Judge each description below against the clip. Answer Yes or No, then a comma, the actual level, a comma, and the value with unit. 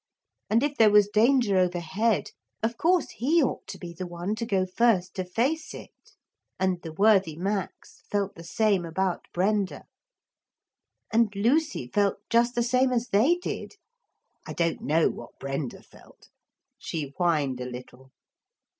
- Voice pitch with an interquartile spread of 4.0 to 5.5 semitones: Yes, average, 5.2 semitones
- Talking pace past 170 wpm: No, average, 155 wpm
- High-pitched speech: Yes, high, 200 Hz